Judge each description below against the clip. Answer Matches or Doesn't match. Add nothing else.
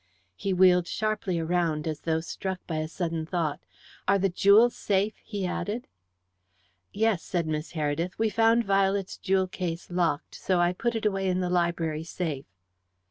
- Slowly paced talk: Doesn't match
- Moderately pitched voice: Matches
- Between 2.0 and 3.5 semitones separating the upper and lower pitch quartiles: Matches